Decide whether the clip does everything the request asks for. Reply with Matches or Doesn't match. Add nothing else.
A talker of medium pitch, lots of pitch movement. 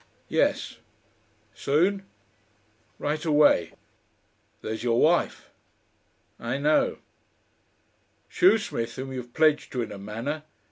Doesn't match